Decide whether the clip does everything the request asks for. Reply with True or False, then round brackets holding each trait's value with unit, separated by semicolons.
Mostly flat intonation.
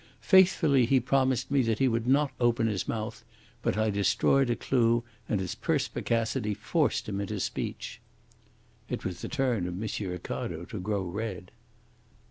False (4.4 semitones)